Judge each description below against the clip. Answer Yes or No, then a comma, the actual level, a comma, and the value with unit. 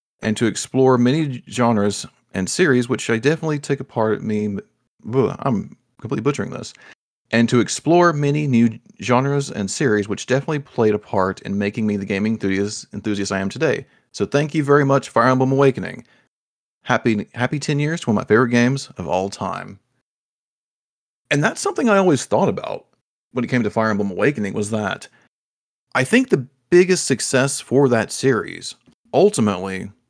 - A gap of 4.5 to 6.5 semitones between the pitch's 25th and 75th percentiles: Yes, average, 5.0 semitones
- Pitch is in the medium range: No, low, 125 Hz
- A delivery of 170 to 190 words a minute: Yes, average, 175 wpm